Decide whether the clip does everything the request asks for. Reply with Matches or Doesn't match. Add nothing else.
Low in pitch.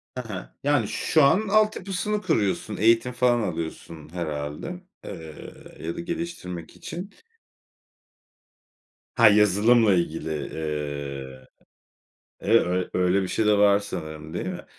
Matches